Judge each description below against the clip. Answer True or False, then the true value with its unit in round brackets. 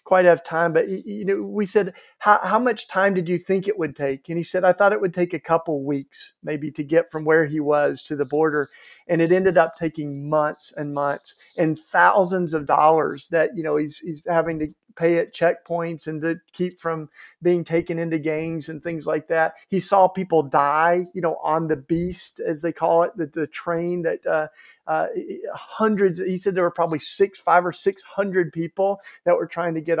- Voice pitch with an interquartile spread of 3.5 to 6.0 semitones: False (2.7 semitones)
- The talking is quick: True (220 wpm)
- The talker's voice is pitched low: False (170 Hz)